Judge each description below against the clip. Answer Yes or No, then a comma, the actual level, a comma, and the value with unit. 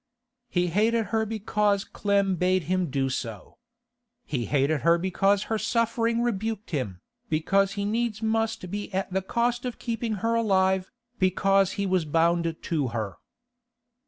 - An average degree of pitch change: Yes, average, 4.7 semitones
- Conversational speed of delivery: Yes, average, 150 wpm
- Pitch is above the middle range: Yes, high, 195 Hz